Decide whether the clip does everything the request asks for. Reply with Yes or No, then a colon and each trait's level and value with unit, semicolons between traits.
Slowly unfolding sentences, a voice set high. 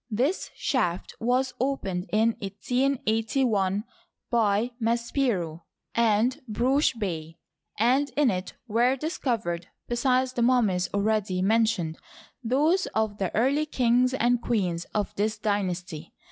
Yes: slow, 115 wpm; high, 225 Hz